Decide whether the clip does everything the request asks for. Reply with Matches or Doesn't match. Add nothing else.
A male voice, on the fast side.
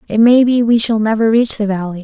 Doesn't match